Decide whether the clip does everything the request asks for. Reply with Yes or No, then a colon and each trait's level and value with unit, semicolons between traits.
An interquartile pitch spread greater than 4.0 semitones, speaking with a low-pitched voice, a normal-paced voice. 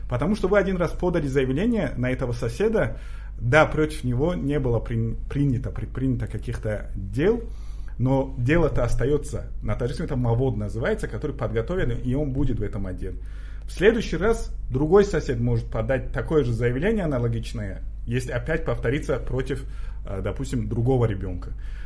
Yes: average, 4.7 semitones; low, 125 Hz; average, 145 wpm